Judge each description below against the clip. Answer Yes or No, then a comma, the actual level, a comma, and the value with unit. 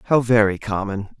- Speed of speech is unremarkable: Yes, average, 150 wpm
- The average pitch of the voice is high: No, low, 110 Hz